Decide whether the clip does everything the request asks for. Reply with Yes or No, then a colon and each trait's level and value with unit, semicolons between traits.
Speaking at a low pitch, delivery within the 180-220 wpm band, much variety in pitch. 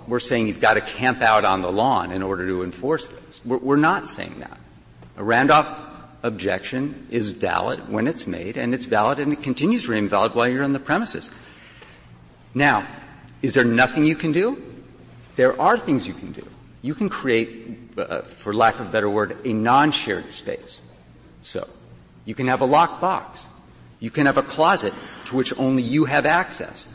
Yes: low, 115 Hz; average, 190 wpm; wide, 6.3 semitones